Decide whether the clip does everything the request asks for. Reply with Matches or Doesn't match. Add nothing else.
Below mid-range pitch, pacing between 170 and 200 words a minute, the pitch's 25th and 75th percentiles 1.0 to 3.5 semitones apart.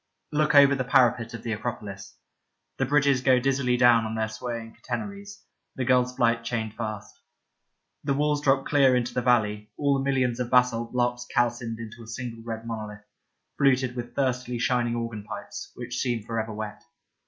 Matches